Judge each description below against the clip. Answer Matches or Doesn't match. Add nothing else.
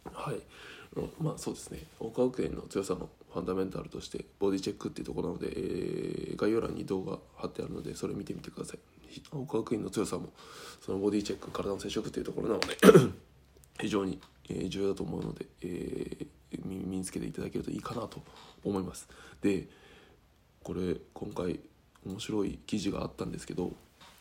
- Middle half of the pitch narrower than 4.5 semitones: Matches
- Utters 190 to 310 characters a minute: Doesn't match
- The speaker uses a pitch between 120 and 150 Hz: Doesn't match